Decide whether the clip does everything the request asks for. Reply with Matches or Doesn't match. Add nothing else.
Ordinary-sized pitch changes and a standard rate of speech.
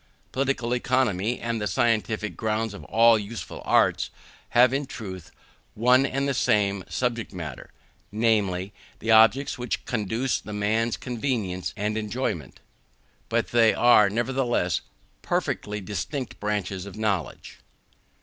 Doesn't match